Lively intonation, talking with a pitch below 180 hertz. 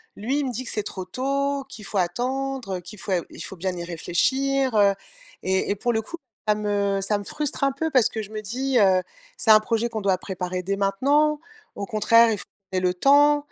No: wide, 5.7 semitones; high, 215 Hz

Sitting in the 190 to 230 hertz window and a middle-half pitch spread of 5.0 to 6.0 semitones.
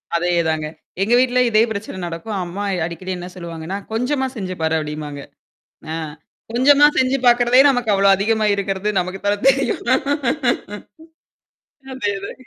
Yes: high, 200 Hz; wide, 5.6 semitones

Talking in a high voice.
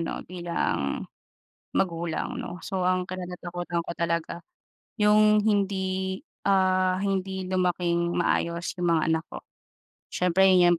No: medium, 180 Hz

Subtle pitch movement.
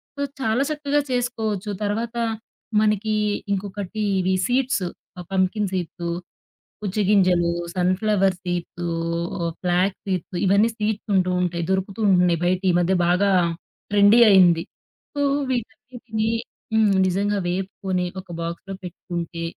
No: average, 3.2 semitones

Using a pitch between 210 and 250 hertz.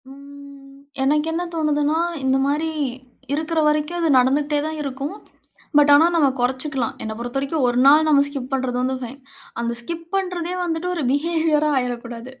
No: very high, 285 Hz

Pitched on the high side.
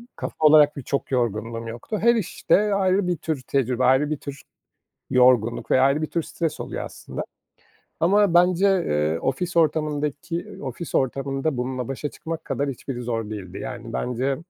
No: medium, 140 Hz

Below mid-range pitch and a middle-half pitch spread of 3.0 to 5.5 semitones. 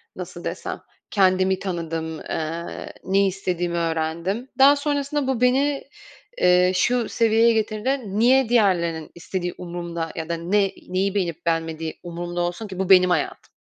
No: medium, 185 Hz; average, 4.7 semitones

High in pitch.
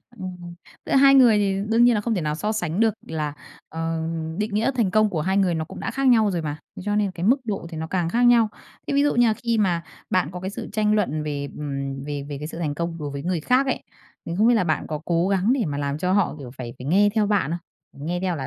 No: medium, 180 Hz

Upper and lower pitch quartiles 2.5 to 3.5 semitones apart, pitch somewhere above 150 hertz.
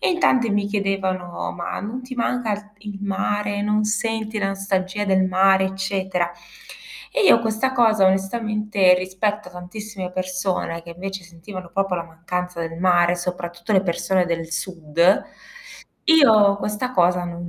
Yes: average, 2.8 semitones; high, 190 Hz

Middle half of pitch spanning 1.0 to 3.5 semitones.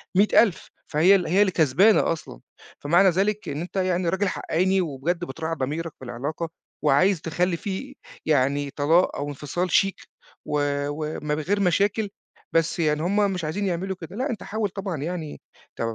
No: average, 4.2 semitones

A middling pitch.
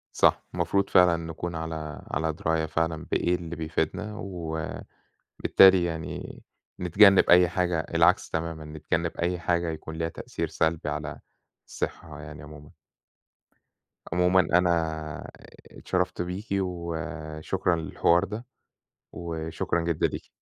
No: very low, 85 Hz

